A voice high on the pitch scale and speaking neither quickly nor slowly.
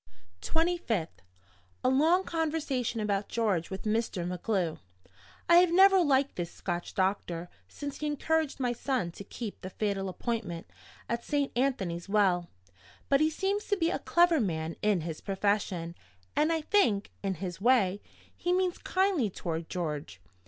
Yes: high, 225 Hz; average, 150 wpm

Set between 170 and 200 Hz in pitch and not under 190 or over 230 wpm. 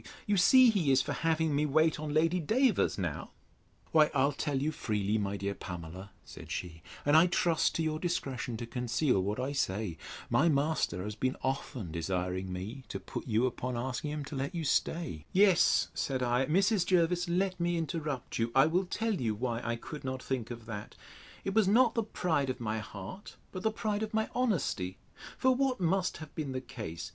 No: medium, 140 Hz; average, 200 wpm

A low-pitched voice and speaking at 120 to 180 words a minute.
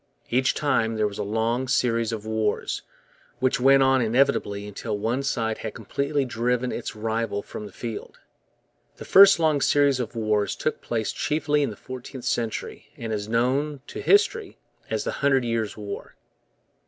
Yes: low, 120 Hz; average, 165 wpm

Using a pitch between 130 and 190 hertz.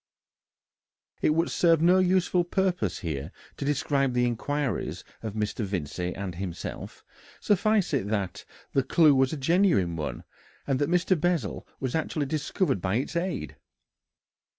Yes: medium, 140 Hz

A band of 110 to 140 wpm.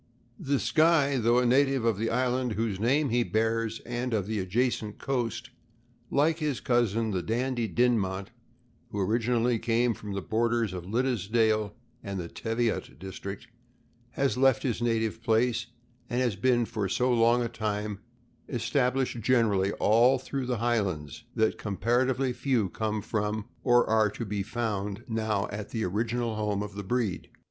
No: average, 160 wpm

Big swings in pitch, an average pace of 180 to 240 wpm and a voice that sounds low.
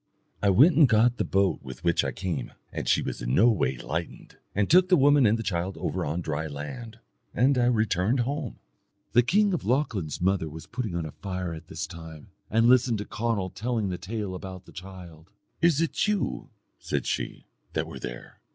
Yes: wide, 6.4 semitones; average, 200 wpm; low, 100 Hz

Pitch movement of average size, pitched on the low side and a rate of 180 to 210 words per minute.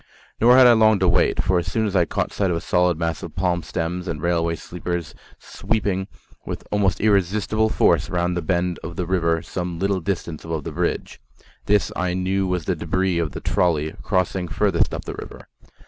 No: narrow, 2.3 semitones; very low, 90 Hz; average, 195 wpm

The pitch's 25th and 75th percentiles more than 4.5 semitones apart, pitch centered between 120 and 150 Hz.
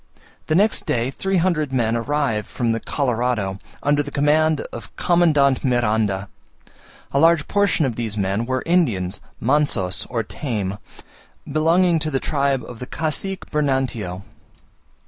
Yes: wide, 5.4 semitones; low, 135 Hz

